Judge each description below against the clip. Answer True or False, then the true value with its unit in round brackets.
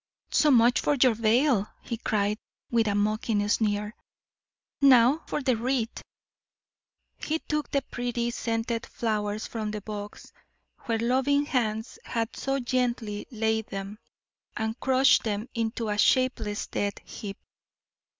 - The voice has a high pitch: True (230 Hz)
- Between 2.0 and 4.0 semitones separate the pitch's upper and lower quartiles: True (3.1 semitones)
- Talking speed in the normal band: False (130 wpm)